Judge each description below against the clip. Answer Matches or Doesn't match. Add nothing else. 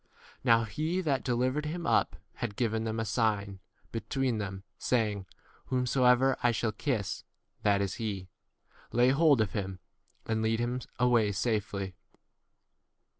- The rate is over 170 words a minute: Doesn't match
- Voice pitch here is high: Doesn't match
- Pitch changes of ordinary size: Matches